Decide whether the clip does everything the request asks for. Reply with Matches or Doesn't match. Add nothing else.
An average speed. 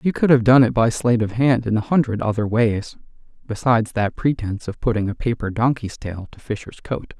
Doesn't match